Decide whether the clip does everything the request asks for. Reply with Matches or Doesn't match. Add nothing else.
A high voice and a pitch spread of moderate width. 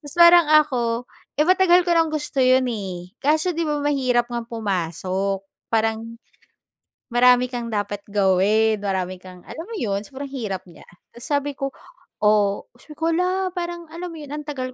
Doesn't match